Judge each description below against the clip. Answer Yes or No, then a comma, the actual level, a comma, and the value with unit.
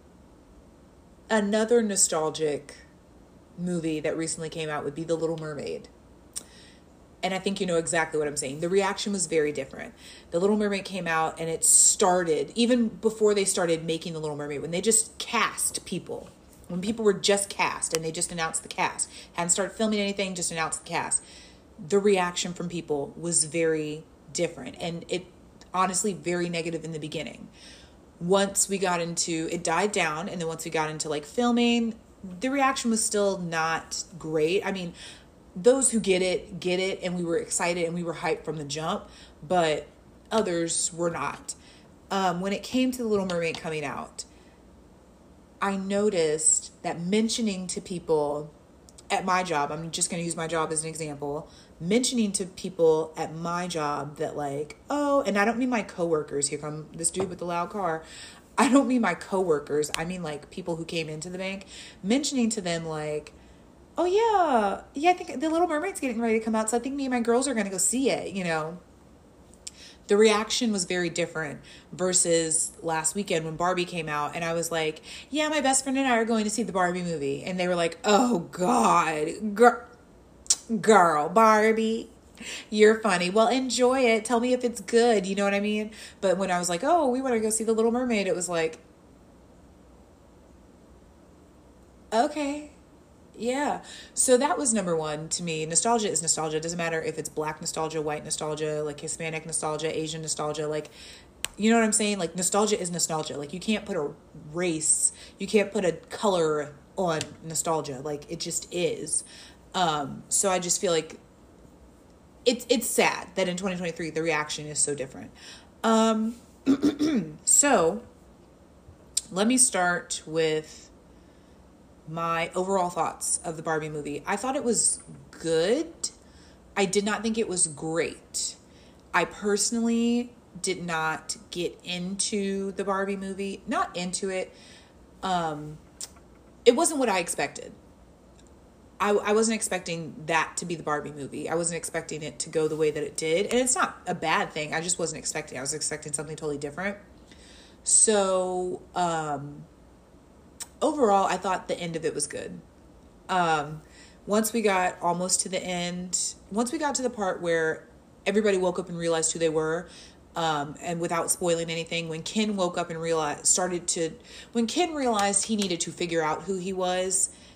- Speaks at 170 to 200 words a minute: Yes, average, 180 wpm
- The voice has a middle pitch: Yes, medium, 180 Hz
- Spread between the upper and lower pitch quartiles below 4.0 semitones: No, average, 4.9 semitones